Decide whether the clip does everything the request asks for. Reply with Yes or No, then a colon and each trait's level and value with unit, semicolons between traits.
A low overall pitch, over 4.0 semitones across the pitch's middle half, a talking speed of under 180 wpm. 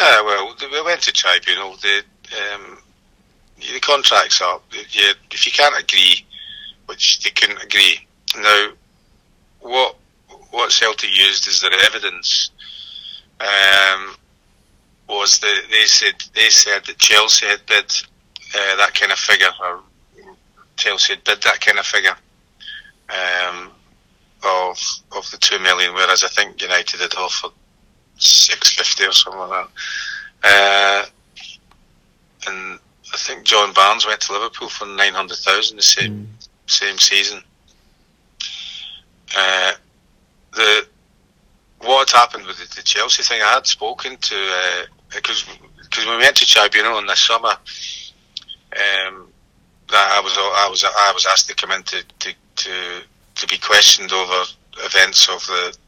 Yes: low, 100 Hz; average, 4.4 semitones; average, 145 wpm